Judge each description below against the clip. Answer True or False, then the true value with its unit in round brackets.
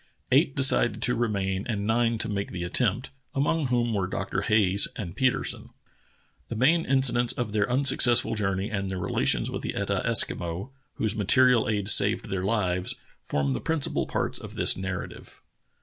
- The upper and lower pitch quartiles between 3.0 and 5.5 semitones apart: True (4.2 semitones)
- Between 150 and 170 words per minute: True (165 wpm)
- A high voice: False (110 Hz)